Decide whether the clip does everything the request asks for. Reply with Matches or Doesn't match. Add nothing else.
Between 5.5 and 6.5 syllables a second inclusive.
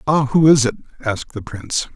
Matches